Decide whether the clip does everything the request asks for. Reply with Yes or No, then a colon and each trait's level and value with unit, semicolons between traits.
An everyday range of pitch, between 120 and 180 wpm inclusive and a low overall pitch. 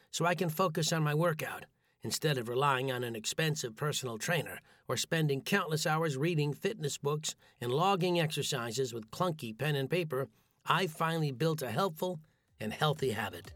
No: average, 4.2 semitones; average, 170 wpm; medium, 150 Hz